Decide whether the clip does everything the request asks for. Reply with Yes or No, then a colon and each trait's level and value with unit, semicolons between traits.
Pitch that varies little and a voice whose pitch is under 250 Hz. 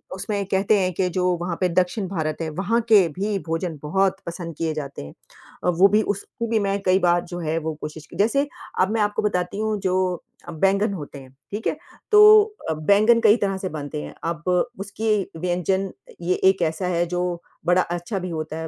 No: average, 3.1 semitones; medium, 185 Hz